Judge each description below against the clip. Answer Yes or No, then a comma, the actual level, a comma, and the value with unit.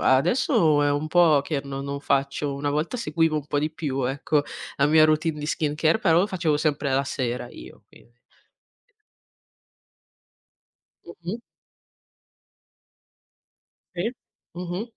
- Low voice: No, medium, 150 Hz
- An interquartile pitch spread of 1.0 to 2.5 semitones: No, average, 2.9 semitones